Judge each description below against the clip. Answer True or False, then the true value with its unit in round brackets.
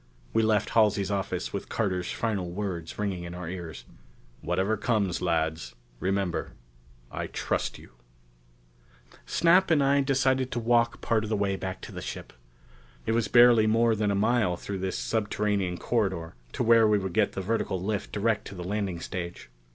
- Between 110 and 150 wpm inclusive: False (175 wpm)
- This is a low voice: True (100 Hz)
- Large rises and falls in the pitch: False (3.6 semitones)